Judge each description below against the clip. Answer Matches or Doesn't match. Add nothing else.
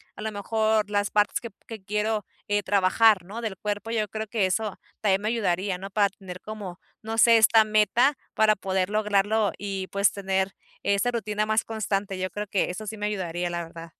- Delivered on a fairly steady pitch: Matches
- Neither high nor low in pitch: Doesn't match